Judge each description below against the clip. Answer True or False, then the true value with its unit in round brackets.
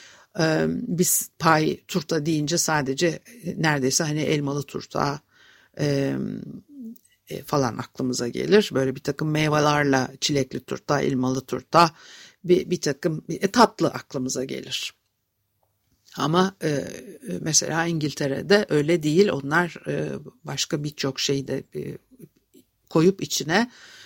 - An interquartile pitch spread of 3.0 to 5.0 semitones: True (4.5 semitones)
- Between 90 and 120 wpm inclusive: True (110 wpm)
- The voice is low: False (150 Hz)